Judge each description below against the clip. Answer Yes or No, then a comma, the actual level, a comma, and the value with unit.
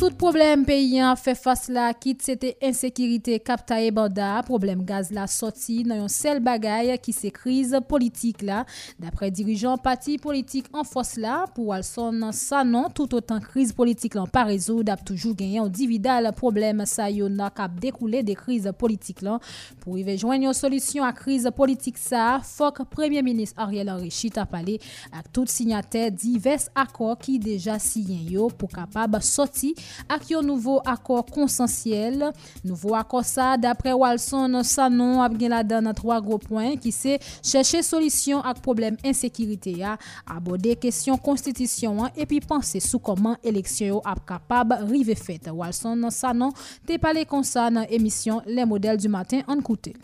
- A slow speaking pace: Yes, slow, 140 wpm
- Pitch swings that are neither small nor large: Yes, average, 3.5 semitones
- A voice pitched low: No, high, 235 Hz